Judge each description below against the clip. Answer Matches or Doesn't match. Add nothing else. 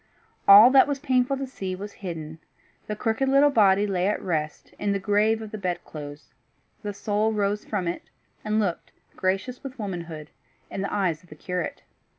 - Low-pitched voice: Doesn't match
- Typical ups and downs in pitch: Matches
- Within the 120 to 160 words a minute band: Doesn't match